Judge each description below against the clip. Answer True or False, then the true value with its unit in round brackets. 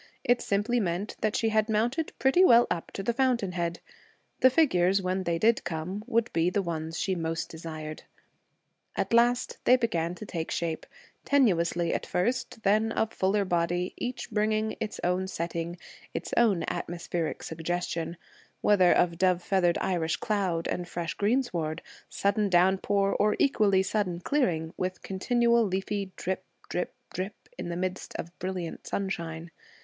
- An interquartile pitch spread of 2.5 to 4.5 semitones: True (4.1 semitones)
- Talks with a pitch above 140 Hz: True (190 Hz)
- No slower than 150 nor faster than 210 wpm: True (155 wpm)